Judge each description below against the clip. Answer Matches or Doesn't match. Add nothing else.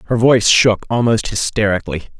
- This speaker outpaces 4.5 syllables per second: Matches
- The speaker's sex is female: Doesn't match